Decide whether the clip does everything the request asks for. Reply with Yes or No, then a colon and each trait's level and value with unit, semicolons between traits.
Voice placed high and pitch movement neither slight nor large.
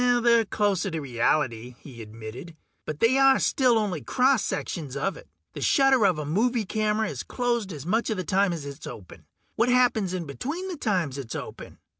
No: high, 195 Hz; wide, 8.4 semitones